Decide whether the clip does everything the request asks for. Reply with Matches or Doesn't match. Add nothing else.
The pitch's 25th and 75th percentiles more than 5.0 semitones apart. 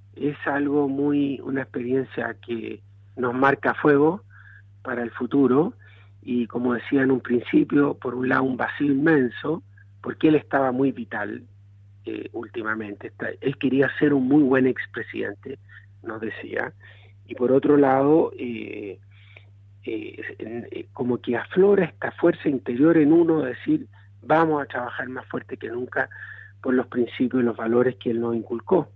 Doesn't match